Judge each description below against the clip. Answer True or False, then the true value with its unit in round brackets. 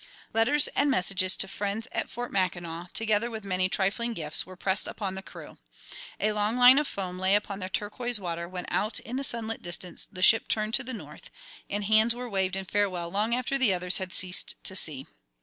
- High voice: True (200 Hz)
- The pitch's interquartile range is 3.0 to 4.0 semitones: True (3.5 semitones)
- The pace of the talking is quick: True (210 wpm)